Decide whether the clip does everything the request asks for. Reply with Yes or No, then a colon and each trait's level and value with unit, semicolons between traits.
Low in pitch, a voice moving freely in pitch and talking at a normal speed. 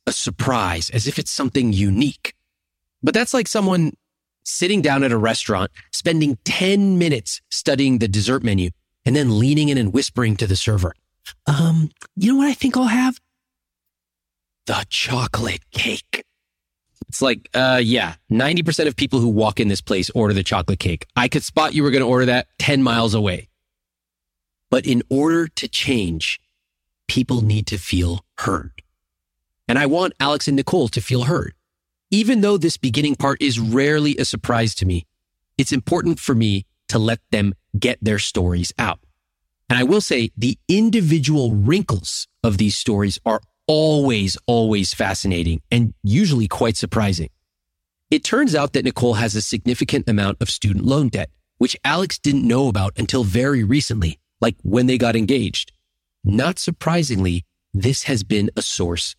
Yes: low, 115 Hz; wide, 6.8 semitones; average, 165 wpm